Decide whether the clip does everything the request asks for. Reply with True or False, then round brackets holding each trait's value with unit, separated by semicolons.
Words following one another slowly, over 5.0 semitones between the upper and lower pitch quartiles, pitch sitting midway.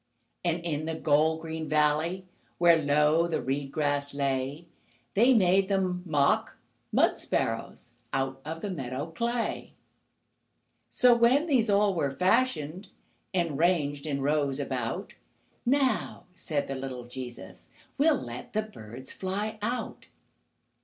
True (130 wpm; 5.4 semitones; 160 Hz)